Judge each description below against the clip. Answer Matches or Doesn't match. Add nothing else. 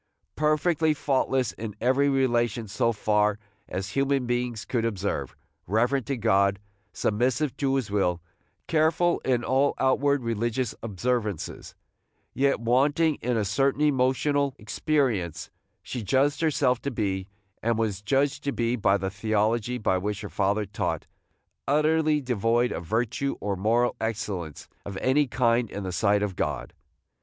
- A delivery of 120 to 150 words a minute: Matches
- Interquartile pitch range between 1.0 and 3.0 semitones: Doesn't match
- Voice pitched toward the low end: Matches